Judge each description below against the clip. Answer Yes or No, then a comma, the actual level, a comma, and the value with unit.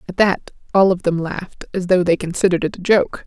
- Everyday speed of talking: No, fast, 240 wpm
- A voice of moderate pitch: Yes, medium, 180 Hz